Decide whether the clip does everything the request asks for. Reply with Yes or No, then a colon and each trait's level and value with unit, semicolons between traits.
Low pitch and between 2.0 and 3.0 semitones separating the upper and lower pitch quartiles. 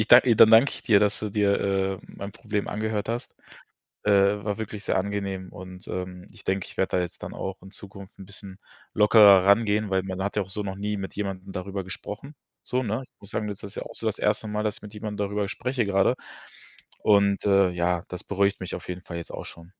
No: low, 100 Hz; narrow, 1.6 semitones